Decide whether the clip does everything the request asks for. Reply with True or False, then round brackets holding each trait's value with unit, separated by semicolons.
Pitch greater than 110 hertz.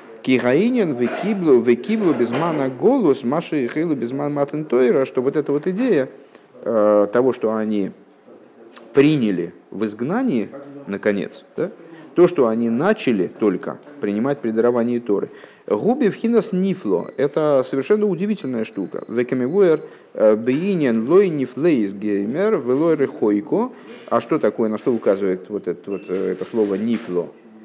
True (125 Hz)